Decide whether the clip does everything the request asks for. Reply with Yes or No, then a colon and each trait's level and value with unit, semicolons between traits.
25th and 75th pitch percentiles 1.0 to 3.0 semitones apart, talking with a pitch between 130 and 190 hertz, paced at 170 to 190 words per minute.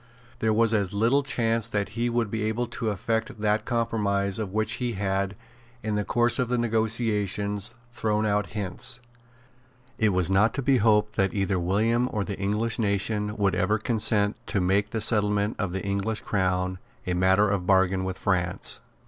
No: narrow, 2.4 semitones; low, 105 Hz; average, 180 wpm